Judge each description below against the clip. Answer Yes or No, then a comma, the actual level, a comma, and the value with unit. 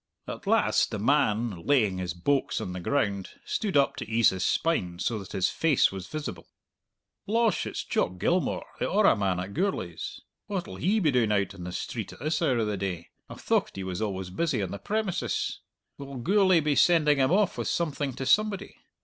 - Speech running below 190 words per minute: No, average, 200 wpm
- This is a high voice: No, low, 125 Hz